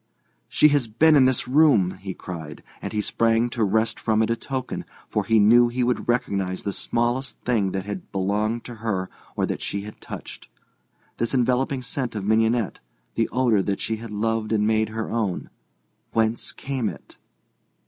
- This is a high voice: No, low, 115 Hz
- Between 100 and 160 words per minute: No, average, 180 wpm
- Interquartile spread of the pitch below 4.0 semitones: Yes, average, 2.8 semitones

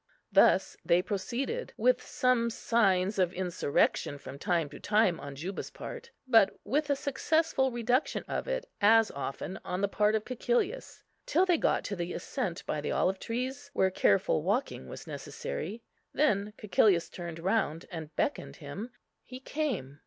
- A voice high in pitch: Yes, high, 210 Hz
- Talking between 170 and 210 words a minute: No, average, 160 wpm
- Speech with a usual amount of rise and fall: No, wide, 6.8 semitones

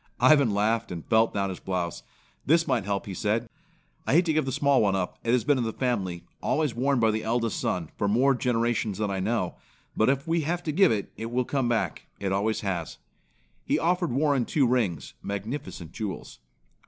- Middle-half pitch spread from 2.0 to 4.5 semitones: No, average, 5.3 semitones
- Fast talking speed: Yes, fast, 210 wpm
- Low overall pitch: Yes, low, 115 Hz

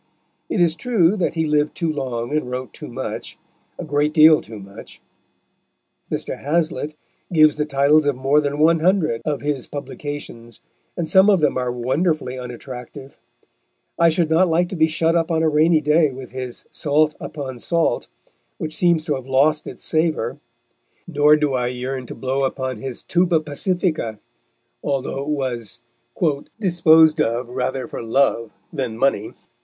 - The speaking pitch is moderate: Yes, medium, 150 Hz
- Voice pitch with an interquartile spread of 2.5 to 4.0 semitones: Yes, average, 3.7 semitones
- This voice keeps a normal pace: Yes, average, 165 wpm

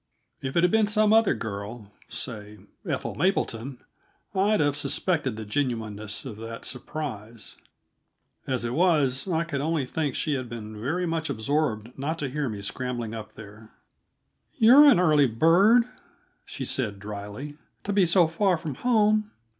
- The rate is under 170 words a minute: Yes, average, 155 wpm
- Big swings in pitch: Yes, wide, 7.1 semitones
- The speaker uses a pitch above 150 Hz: No, medium, 140 Hz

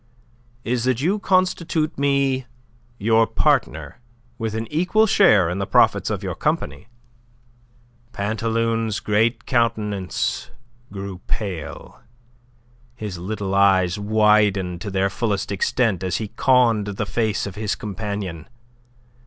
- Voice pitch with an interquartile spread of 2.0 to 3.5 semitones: Yes, average, 3.2 semitones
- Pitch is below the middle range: Yes, low, 105 Hz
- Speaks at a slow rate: Yes, slow, 120 wpm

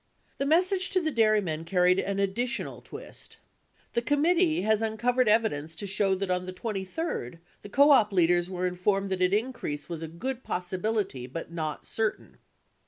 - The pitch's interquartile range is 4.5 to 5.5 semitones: Yes, average, 5.2 semitones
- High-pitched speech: Yes, high, 200 Hz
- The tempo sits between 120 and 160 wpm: No, average, 170 wpm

